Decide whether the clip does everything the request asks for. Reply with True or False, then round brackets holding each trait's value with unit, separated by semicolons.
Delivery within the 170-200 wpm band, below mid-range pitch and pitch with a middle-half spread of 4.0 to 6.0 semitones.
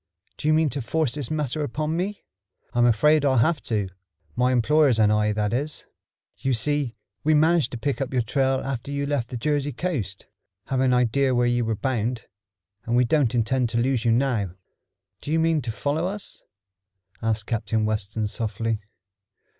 True (185 wpm; 130 Hz; 4.4 semitones)